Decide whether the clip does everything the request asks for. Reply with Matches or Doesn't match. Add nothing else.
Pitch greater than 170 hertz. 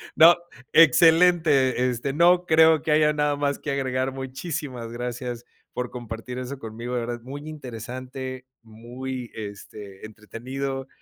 Doesn't match